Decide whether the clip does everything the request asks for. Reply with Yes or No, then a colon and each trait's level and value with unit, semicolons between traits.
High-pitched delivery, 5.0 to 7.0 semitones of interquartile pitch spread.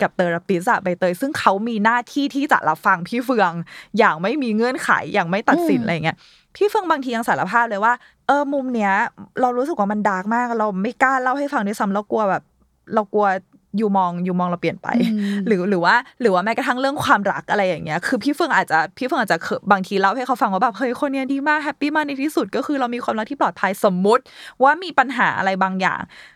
Yes: high, 230 Hz; wide, 5.6 semitones